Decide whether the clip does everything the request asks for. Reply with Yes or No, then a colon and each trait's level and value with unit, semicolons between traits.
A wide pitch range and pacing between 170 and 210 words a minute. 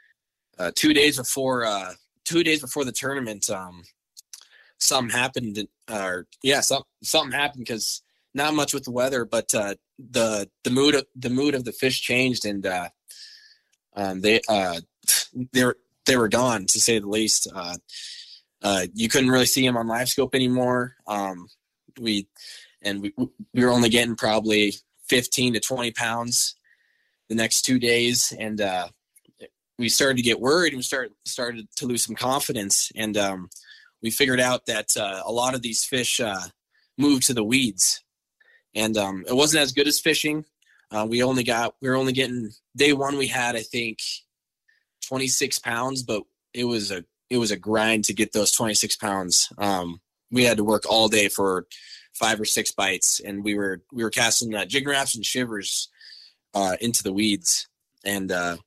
No: average, 3.5 semitones; average, 180 wpm